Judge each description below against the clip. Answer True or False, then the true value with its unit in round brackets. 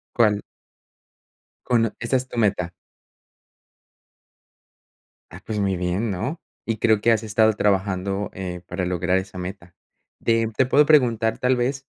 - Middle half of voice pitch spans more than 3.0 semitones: True (3.8 semitones)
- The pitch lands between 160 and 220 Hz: False (105 Hz)